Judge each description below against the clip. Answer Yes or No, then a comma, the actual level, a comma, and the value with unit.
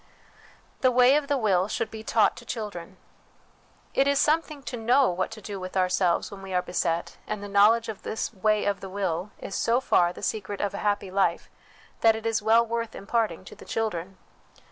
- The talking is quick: Yes, fast, 210 wpm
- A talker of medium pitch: No, high, 210 Hz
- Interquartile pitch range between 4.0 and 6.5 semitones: No, average, 3.4 semitones